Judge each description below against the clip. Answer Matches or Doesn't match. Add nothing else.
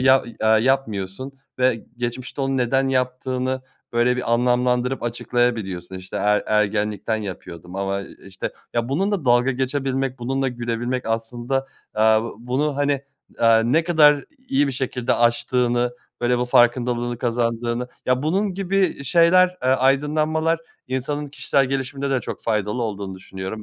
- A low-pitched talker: Matches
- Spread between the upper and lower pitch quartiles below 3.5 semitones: Matches